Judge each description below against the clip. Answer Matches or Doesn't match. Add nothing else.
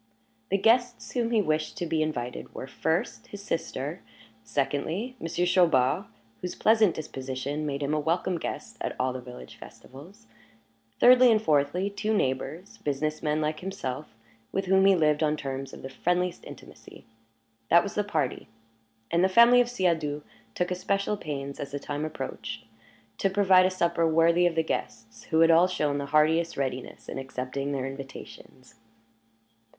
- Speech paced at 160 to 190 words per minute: Matches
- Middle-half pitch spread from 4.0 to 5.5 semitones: Matches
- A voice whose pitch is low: Doesn't match